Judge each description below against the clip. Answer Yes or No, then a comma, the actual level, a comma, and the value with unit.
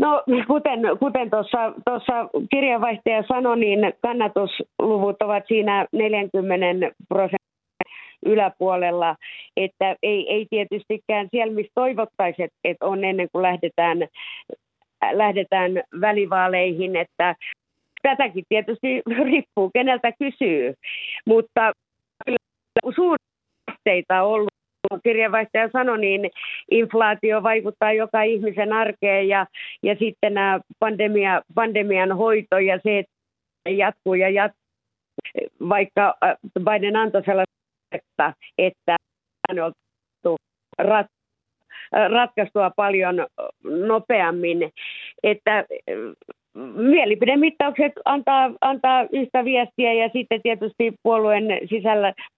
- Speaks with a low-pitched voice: No, high, 215 Hz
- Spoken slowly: Yes, slow, 90 wpm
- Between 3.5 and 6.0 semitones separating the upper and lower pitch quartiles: Yes, average, 3.9 semitones